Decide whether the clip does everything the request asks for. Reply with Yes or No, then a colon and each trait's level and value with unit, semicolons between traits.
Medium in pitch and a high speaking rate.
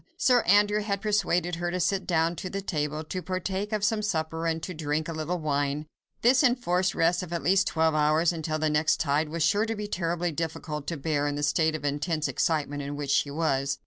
Yes: medium, 165 Hz; fast, 225 wpm